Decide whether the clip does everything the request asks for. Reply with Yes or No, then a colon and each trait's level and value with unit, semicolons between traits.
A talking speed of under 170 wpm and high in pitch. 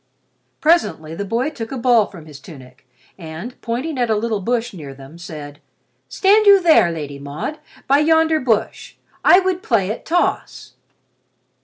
Yes: average, 160 wpm; high, 225 Hz